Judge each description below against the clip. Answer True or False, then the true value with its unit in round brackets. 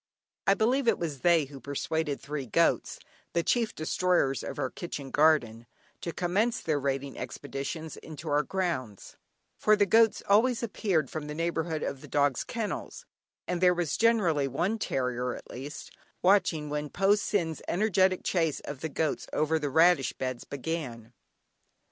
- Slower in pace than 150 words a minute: False (160 wpm)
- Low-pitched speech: False (160 Hz)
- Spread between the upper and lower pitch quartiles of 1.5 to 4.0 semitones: False (5.0 semitones)